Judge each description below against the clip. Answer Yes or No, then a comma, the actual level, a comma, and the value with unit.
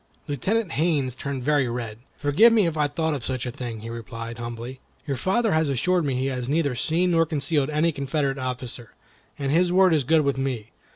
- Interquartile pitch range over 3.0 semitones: Yes, average, 4.2 semitones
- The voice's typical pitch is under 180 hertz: Yes, medium, 140 Hz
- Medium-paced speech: No, fast, 210 wpm